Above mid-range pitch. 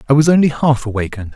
No: low, 135 Hz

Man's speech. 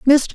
No: female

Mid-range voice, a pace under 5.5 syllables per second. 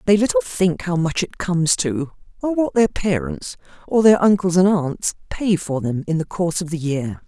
Yes: medium, 170 Hz; 5.0 syllables/s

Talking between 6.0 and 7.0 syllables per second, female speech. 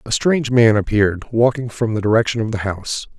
No: 6.2 syllables/s; male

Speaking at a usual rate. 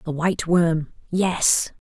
No: slow, 95 wpm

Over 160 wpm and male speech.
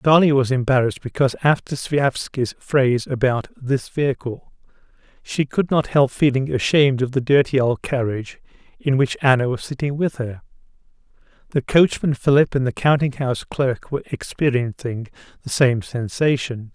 No: average, 145 wpm; male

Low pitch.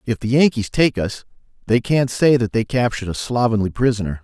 Yes: low, 120 Hz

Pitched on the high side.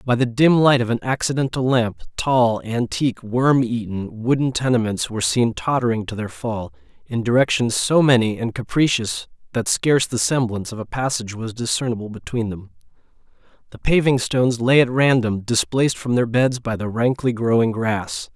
No: low, 120 Hz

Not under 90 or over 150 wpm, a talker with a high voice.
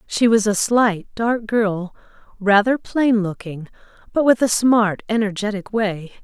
Yes: average, 145 wpm; high, 215 Hz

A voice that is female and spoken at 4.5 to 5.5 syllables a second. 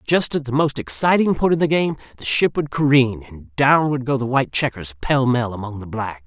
No: male; 5.3 syllables/s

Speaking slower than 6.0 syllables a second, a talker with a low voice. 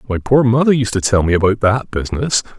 No: 6.1 syllables/s; low, 115 Hz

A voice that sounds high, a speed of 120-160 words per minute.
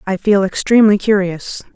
Yes: high, 200 Hz; slow, 135 wpm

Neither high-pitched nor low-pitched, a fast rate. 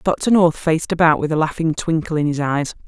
Yes: medium, 160 Hz; fast, 230 wpm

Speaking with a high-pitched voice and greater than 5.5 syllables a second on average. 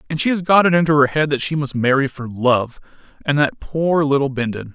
No: medium, 145 Hz; 5.7 syllables/s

